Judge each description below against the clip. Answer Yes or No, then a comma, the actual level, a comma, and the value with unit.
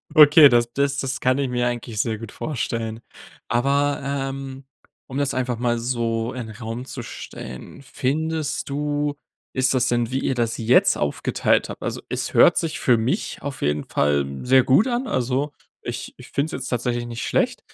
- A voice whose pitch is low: Yes, low, 130 Hz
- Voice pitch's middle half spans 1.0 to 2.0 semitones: No, average, 2.9 semitones